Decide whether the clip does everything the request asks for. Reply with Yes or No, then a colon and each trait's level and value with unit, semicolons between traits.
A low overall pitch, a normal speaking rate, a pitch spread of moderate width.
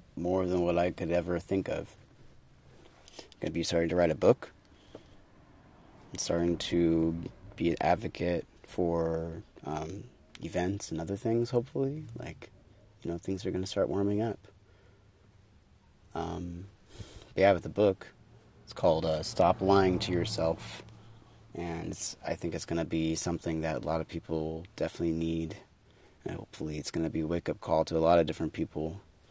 Yes: very low, 90 Hz; average, 160 wpm; average, 3.3 semitones